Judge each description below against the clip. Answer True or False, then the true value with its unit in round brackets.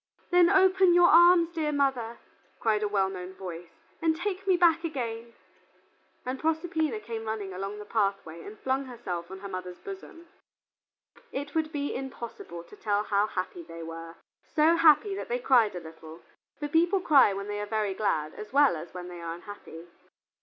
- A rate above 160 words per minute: True (180 wpm)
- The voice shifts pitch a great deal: True (8.9 semitones)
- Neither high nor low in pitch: False (225 Hz)